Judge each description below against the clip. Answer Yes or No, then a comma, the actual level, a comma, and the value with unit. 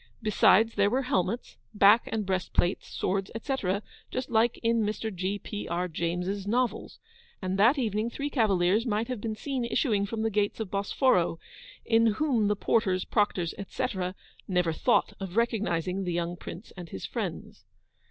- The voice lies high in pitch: Yes, high, 205 Hz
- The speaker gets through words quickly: No, average, 165 wpm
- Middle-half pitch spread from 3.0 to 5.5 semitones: Yes, average, 3.7 semitones